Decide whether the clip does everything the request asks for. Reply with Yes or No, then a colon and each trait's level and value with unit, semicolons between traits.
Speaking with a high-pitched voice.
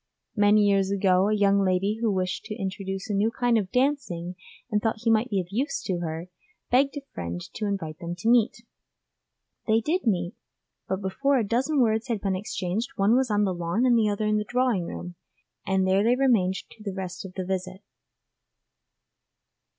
Yes: high, 205 Hz